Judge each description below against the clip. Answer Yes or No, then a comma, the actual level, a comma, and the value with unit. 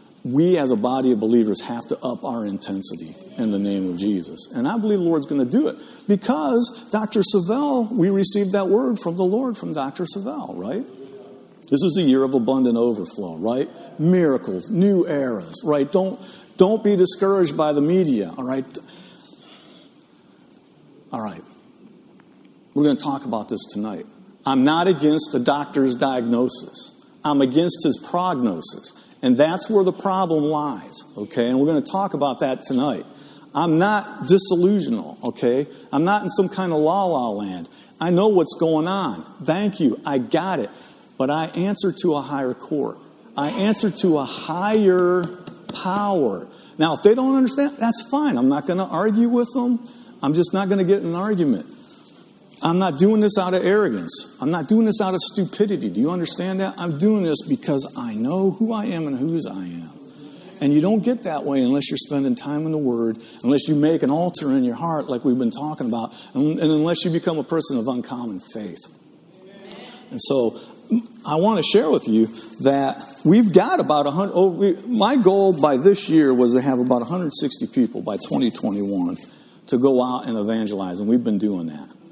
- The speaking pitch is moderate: Yes, medium, 175 Hz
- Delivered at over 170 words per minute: Yes, average, 185 wpm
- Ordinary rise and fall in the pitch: No, wide, 6.7 semitones